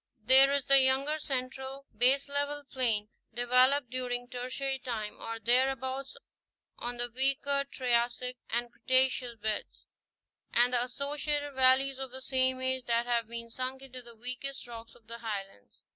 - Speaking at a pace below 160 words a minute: Yes, average, 150 wpm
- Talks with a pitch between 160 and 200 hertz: No, very high, 255 Hz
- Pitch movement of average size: No, narrow, 2.1 semitones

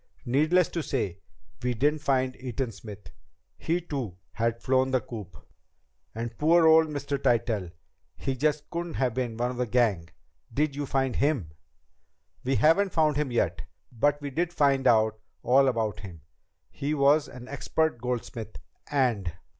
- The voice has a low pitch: Yes, low, 130 Hz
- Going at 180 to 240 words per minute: No, average, 155 wpm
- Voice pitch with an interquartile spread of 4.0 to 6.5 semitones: Yes, average, 4.3 semitones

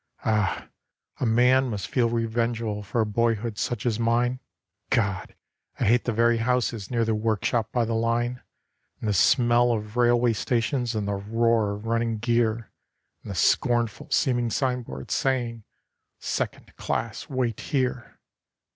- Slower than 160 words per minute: Yes, average, 145 wpm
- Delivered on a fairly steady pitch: Yes, narrow, 1.7 semitones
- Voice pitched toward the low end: Yes, low, 115 Hz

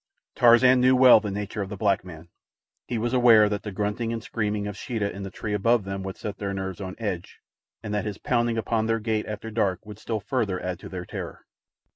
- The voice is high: No, low, 105 Hz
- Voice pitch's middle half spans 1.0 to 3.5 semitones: Yes, average, 2.7 semitones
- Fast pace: Yes, fast, 230 wpm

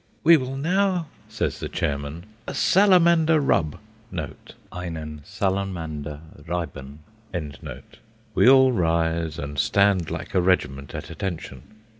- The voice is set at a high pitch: No, very low, 90 Hz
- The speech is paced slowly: Yes, slow, 110 wpm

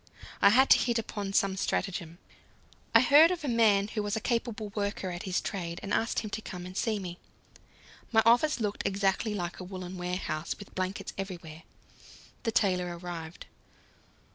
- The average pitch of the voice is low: No, high, 200 Hz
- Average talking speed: Yes, average, 175 wpm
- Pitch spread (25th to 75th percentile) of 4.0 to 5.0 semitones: No, average, 3.6 semitones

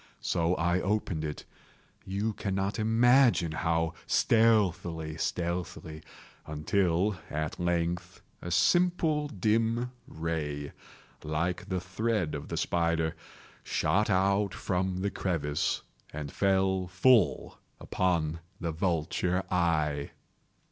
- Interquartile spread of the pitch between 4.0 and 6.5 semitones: No, average, 3.5 semitones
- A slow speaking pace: Yes, slow, 95 wpm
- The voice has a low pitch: Yes, very low, 90 Hz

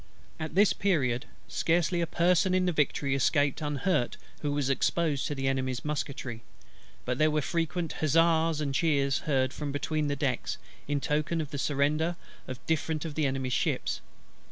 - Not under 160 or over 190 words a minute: Yes, average, 170 wpm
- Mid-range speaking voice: Yes, medium, 150 Hz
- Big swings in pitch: No, average, 3.2 semitones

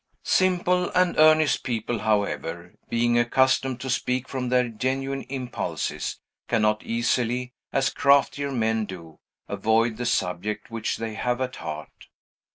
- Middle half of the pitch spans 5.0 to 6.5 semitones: No, average, 3.3 semitones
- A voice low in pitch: Yes, low, 120 Hz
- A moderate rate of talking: No, slow, 130 wpm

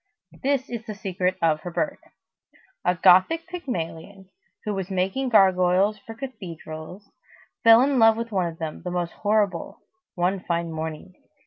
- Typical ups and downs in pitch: Yes, average, 4.3 semitones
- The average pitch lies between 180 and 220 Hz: Yes, high, 190 Hz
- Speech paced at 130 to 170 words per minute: Yes, average, 150 wpm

